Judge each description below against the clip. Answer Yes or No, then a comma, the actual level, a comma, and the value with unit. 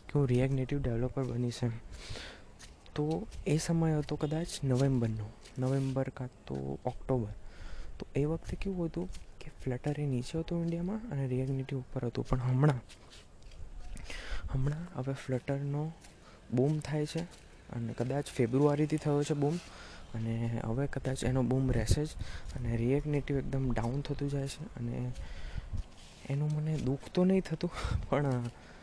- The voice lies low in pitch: Yes, low, 130 Hz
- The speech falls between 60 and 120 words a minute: No, average, 135 wpm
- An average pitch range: Yes, average, 3.8 semitones